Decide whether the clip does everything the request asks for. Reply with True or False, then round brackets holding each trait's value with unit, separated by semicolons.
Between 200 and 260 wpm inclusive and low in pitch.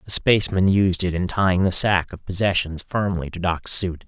True (205 wpm; 90 Hz)